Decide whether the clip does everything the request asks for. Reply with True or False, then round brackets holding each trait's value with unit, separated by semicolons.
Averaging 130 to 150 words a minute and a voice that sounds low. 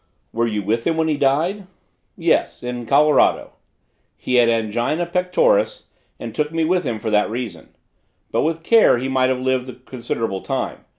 False (175 wpm; 130 Hz)